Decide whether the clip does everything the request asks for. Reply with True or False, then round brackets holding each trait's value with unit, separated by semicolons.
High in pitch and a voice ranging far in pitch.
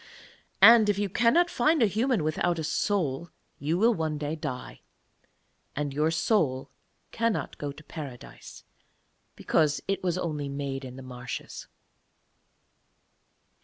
False (160 Hz; 6.4 semitones)